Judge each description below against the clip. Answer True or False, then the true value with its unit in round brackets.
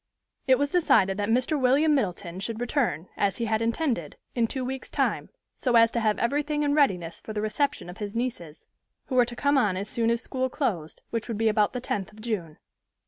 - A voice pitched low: False (230 Hz)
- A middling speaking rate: False (220 wpm)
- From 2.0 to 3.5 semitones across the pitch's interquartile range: False (4.3 semitones)